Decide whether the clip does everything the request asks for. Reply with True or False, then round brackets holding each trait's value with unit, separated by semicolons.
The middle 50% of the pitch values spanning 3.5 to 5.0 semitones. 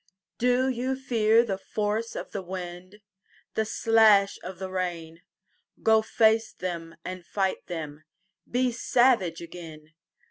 True (4.3 semitones)